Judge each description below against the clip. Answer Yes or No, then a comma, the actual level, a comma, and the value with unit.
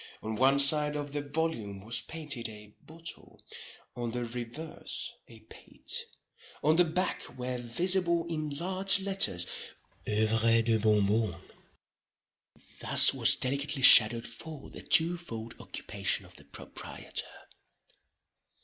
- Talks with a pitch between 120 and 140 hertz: Yes, low, 135 Hz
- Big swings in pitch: Yes, wide, 6.1 semitones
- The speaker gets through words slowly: Yes, slow, 125 wpm